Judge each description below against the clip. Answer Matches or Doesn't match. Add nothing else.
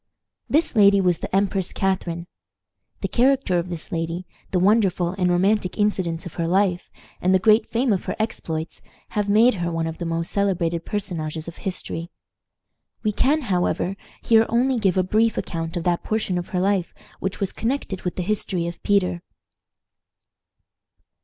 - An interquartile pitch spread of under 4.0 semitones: Matches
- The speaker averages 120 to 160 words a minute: Doesn't match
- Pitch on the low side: Doesn't match